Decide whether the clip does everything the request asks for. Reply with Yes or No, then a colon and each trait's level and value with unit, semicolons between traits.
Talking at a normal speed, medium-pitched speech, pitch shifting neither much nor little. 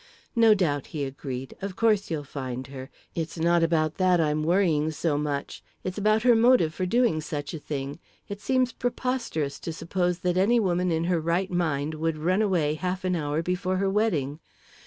Yes: average, 190 wpm; medium, 170 Hz; average, 4.2 semitones